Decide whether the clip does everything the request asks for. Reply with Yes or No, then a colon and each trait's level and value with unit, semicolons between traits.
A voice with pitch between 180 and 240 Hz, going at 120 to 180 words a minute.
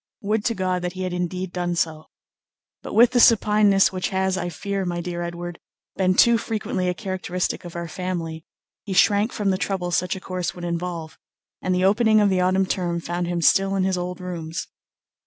No: medium, 185 Hz; fast, 205 wpm